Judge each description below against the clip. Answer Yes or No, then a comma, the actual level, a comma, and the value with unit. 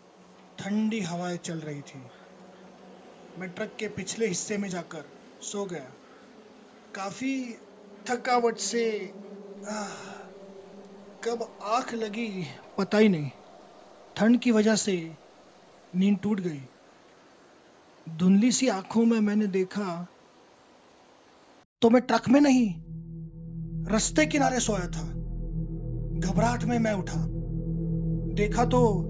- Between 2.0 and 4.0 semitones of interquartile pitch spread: No, average, 5.1 semitones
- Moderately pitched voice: No, high, 200 Hz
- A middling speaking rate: No, slow, 105 wpm